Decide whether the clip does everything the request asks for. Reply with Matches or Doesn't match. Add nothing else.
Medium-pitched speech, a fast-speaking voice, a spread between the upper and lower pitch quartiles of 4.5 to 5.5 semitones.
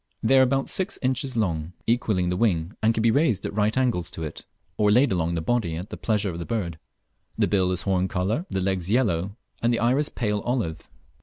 Doesn't match